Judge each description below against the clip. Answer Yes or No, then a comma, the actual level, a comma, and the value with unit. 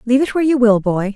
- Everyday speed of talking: No, fast, 310 wpm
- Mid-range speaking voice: No, high, 240 Hz